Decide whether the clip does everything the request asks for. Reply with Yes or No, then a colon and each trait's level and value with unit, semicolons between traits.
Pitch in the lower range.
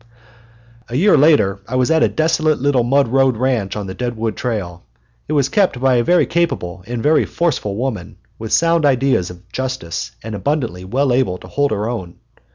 Yes: low, 125 Hz